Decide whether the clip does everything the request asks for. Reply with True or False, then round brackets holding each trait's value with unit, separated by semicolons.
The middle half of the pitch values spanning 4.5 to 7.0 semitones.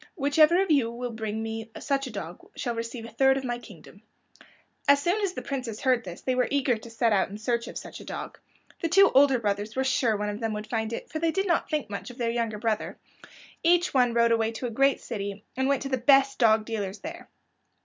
False (3.8 semitones)